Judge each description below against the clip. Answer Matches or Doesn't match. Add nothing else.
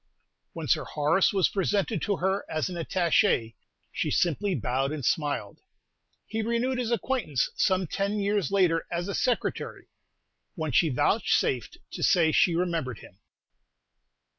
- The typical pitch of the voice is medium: Matches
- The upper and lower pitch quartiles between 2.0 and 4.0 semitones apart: Doesn't match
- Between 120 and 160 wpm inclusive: Matches